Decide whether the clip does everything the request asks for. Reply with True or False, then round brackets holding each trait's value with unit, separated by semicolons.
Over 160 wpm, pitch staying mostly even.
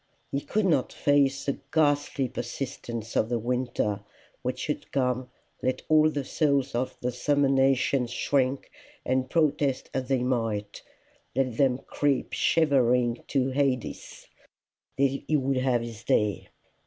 False (135 wpm; 2.2 semitones)